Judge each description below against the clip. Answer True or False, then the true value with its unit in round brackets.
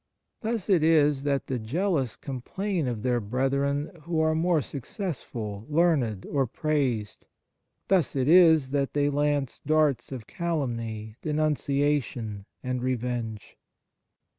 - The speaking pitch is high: False (140 Hz)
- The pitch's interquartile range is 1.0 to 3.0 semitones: False (4.3 semitones)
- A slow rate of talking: True (130 wpm)